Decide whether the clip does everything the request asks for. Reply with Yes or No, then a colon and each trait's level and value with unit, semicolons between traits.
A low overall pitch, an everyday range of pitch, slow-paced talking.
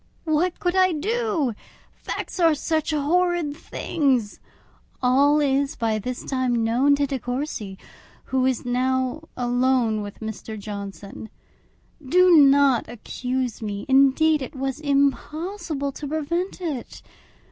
No: very high, 275 Hz; average, 4.1 semitones; slow, 125 wpm